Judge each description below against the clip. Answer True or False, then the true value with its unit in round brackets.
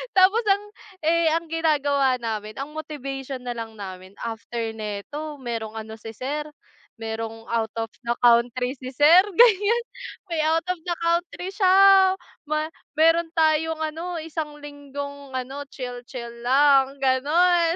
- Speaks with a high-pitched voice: True (280 Hz)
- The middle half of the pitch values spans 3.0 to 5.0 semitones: False (5.4 semitones)